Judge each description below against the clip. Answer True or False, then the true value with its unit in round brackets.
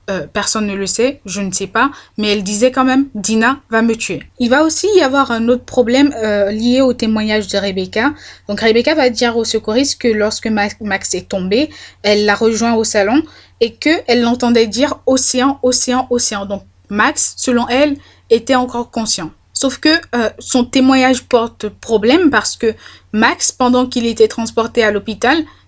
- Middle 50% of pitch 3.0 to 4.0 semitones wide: True (3.3 semitones)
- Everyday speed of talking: True (180 wpm)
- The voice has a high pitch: True (235 Hz)